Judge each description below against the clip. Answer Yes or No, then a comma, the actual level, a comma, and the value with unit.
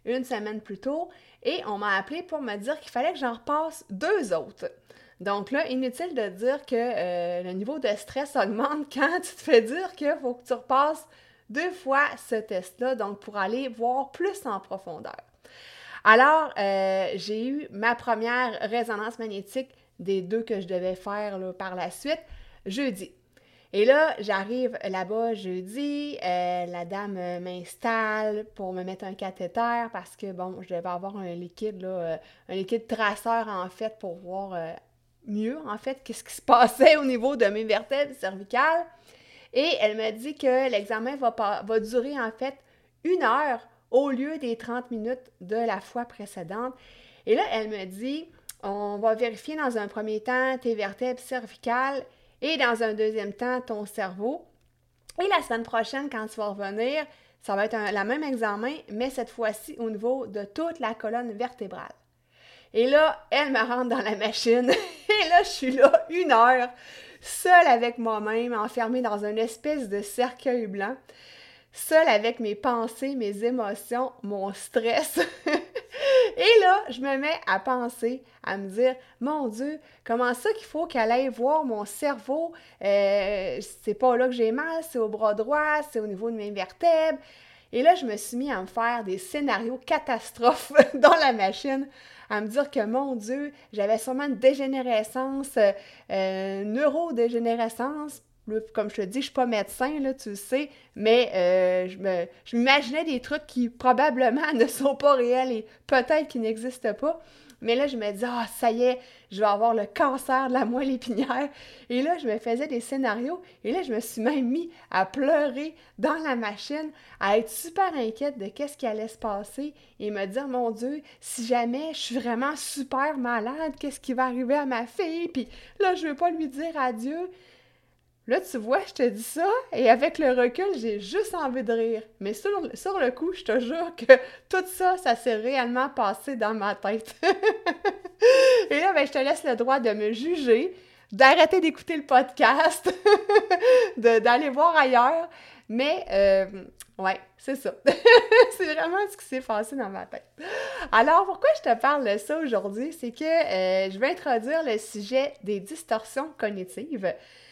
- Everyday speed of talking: Yes, average, 180 wpm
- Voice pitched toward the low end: No, very high, 250 Hz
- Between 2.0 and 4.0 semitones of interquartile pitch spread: No, average, 5.2 semitones